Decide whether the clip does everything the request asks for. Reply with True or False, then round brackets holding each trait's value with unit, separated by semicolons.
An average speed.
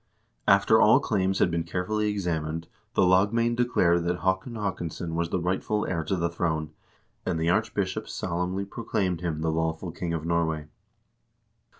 True (160 wpm)